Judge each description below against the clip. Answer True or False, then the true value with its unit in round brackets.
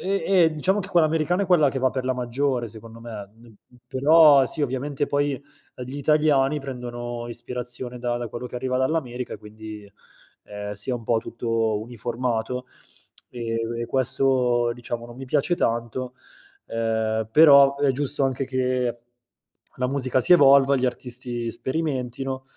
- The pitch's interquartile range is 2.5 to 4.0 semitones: True (2.8 semitones)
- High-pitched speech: False (125 Hz)